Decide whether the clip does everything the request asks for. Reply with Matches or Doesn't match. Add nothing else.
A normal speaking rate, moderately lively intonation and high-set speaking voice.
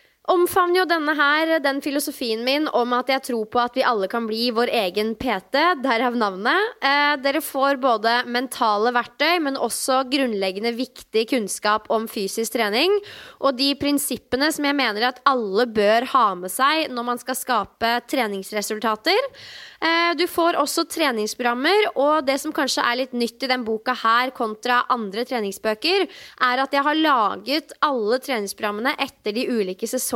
Matches